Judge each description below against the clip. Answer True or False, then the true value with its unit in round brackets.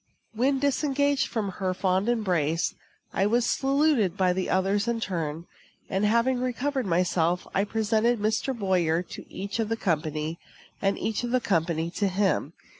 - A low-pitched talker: False (200 Hz)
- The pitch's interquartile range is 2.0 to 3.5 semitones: False (4.9 semitones)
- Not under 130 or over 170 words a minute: True (160 wpm)